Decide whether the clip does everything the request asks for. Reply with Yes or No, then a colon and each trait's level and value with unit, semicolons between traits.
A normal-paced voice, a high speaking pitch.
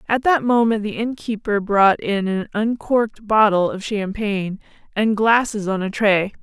Yes: average, 160 wpm; high, 210 Hz